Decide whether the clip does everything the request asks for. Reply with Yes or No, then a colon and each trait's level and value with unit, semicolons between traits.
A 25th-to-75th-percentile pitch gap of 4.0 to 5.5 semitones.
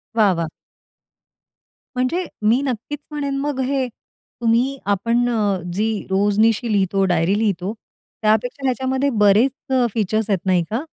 Yes: average, 4.4 semitones